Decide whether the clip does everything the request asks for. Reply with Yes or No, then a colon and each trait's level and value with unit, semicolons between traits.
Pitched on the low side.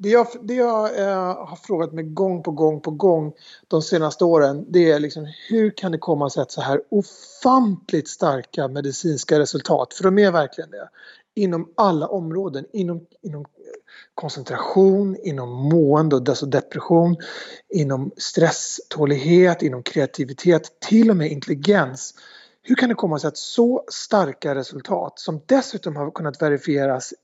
No: medium, 165 Hz